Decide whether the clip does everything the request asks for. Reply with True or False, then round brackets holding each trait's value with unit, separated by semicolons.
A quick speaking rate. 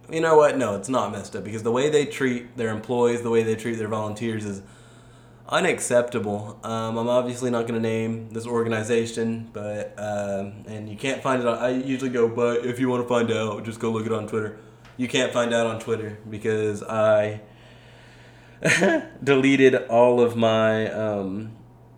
False (190 wpm)